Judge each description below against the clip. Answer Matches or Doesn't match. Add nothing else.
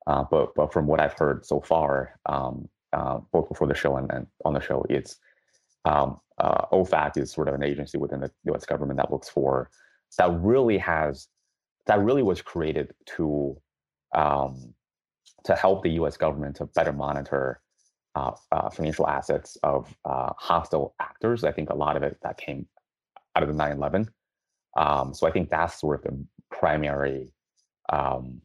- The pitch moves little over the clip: Matches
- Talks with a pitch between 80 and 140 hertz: Doesn't match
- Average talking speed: Matches